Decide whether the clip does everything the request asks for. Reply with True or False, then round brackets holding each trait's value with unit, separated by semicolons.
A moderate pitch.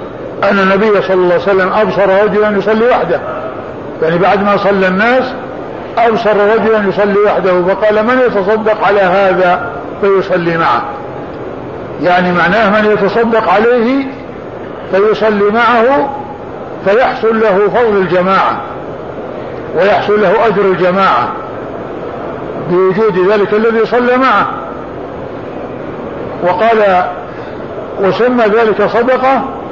False (210 Hz)